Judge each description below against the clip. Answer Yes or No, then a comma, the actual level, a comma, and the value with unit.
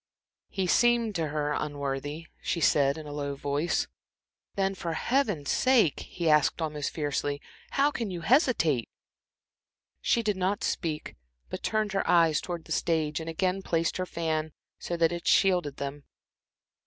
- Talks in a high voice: No, medium, 165 Hz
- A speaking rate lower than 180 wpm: Yes, average, 155 wpm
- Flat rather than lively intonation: No, average, 4.6 semitones